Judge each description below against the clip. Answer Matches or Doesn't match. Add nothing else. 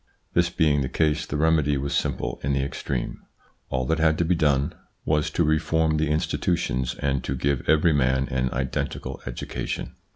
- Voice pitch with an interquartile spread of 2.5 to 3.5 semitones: Matches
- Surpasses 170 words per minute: Matches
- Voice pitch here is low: Matches